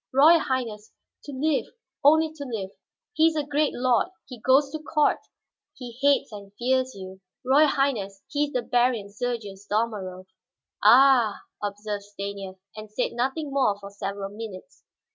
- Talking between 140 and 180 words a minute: Yes, average, 155 wpm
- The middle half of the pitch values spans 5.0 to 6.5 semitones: Yes, wide, 5.4 semitones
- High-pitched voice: Yes, high, 240 Hz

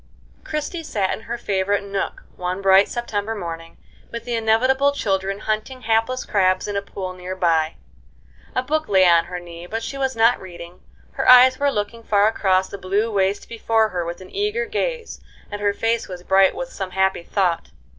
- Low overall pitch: No, high, 205 Hz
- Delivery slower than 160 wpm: No, average, 190 wpm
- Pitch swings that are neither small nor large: Yes, average, 3.9 semitones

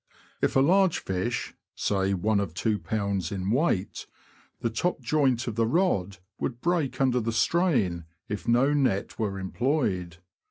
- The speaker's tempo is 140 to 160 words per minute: Yes, average, 145 wpm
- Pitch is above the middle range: No, low, 115 Hz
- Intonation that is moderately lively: No, wide, 5.8 semitones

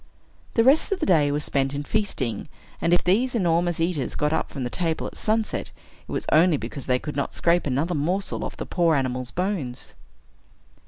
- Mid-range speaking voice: Yes, medium, 165 Hz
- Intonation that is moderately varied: Yes, average, 4.7 semitones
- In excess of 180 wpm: Yes, average, 195 wpm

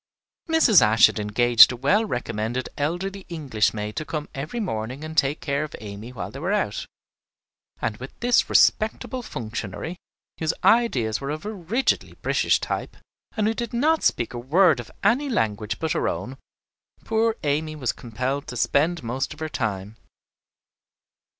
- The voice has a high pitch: No, medium, 140 Hz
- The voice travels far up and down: Yes, wide, 8.8 semitones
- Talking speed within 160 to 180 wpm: Yes, average, 165 wpm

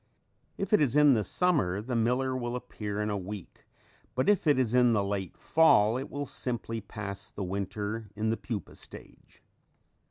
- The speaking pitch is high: No, low, 115 Hz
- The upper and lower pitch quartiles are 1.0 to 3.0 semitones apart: No, average, 4.1 semitones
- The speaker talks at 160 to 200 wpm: Yes, average, 185 wpm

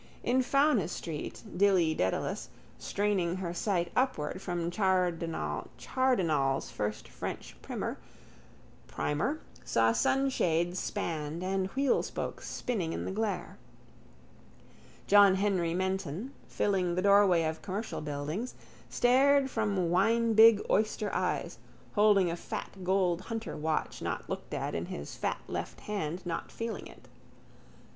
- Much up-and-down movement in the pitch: No, average, 4.3 semitones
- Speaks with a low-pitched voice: No, high, 190 Hz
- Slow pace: Yes, slow, 115 wpm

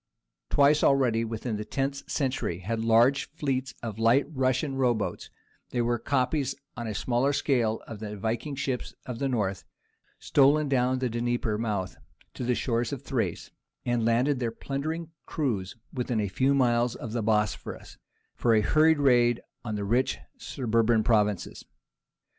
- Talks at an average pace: Yes, average, 155 wpm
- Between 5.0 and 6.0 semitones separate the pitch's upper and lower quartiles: No, average, 3.3 semitones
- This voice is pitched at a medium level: No, low, 120 Hz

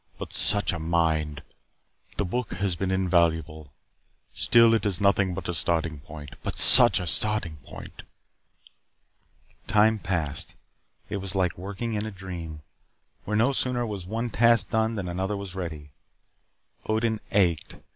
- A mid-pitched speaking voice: No, very low, 95 Hz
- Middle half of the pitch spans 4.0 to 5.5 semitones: Yes, average, 4.3 semitones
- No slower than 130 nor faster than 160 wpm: Yes, average, 145 wpm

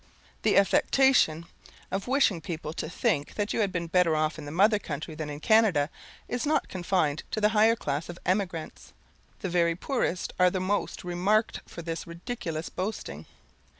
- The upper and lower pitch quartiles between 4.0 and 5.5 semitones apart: Yes, average, 4.4 semitones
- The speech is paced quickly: No, average, 175 wpm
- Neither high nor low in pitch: Yes, medium, 180 Hz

